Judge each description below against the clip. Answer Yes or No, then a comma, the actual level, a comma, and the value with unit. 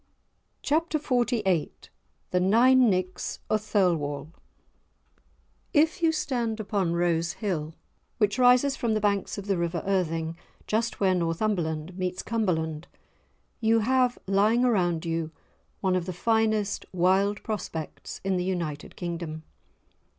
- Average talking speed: No, slow, 125 wpm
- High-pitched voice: Yes, high, 195 Hz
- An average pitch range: Yes, average, 4.7 semitones